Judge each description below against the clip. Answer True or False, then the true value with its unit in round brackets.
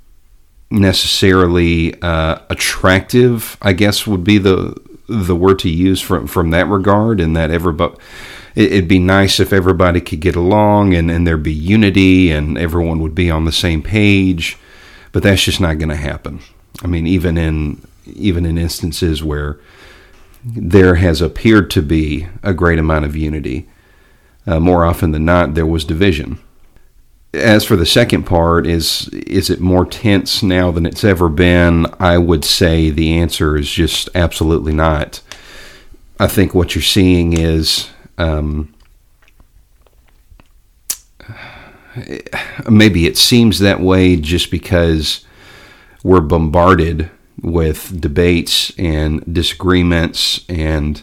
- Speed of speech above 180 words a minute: False (140 wpm)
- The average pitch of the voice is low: True (85 Hz)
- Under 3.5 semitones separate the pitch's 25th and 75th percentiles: True (2.9 semitones)